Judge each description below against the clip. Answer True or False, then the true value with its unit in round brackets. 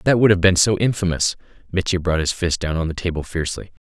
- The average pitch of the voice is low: True (90 Hz)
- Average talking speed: False (250 wpm)